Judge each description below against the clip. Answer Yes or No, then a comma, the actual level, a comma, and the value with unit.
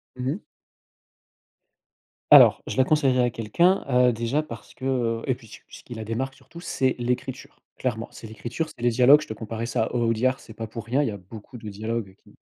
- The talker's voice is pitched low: Yes, low, 120 Hz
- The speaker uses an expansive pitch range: No, average, 2.7 semitones